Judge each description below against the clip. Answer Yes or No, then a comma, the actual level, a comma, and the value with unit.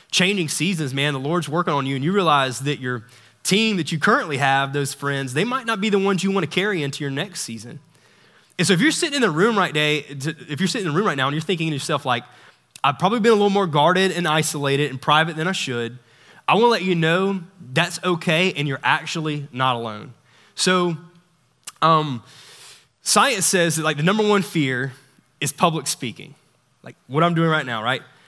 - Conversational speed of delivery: No, fast, 225 wpm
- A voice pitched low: No, medium, 155 Hz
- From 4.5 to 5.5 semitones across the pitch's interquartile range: Yes, average, 5.0 semitones